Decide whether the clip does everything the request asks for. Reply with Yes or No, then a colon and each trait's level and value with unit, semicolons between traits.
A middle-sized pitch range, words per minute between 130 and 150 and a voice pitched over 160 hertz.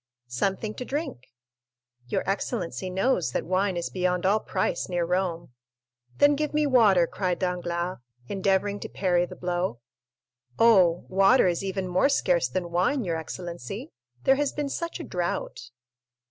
Yes: average, 3.5 semitones; average, 145 wpm; medium, 185 Hz